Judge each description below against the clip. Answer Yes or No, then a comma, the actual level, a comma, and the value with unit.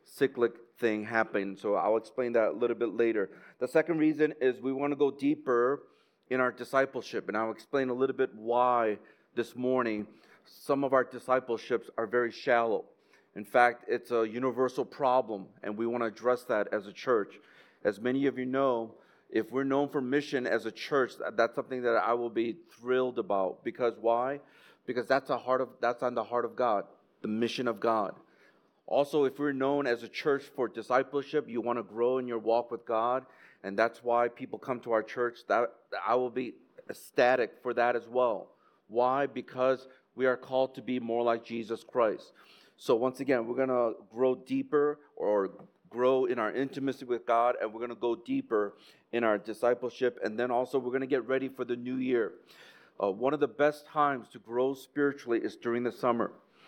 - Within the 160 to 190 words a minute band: No, average, 200 wpm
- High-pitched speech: No, low, 125 Hz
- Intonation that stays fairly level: Yes, narrow, 2.3 semitones